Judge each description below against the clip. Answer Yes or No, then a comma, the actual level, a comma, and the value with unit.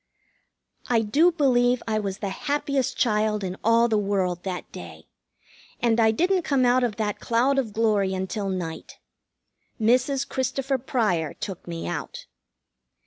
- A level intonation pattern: No, average, 4.6 semitones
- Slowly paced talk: No, average, 145 wpm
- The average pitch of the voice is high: Yes, high, 220 Hz